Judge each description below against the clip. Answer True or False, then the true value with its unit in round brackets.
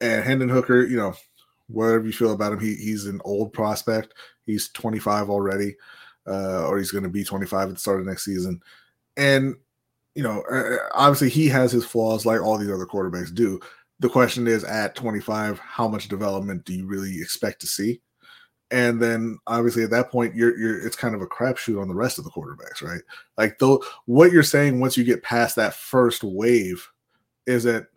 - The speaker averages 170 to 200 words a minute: True (195 wpm)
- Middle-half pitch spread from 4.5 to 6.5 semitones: False (3.3 semitones)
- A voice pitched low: True (115 Hz)